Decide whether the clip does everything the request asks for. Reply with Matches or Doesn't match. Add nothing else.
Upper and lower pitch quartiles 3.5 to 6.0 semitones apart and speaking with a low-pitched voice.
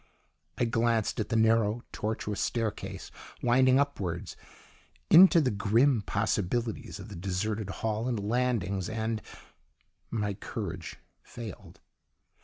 Doesn't match